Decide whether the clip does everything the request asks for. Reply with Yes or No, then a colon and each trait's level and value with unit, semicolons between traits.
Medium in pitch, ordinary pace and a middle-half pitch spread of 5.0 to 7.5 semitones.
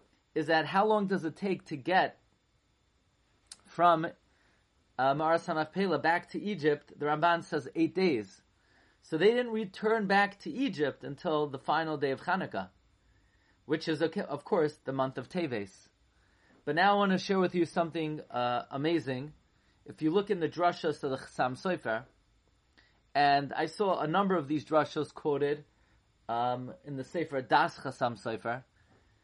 Yes: medium, 155 Hz; average, 160 wpm; average, 5.3 semitones